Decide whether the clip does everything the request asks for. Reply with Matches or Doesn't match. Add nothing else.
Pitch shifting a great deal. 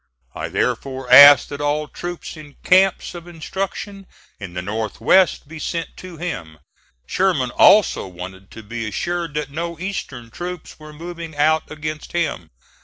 Matches